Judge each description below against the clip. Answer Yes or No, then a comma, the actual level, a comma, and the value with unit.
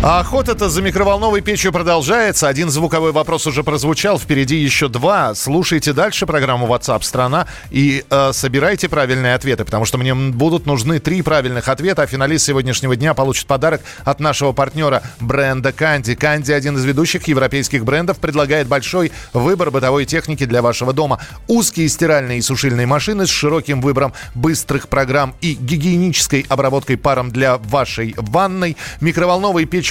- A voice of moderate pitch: Yes, medium, 145 Hz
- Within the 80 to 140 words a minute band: No, average, 155 wpm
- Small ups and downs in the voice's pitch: No, average, 3.6 semitones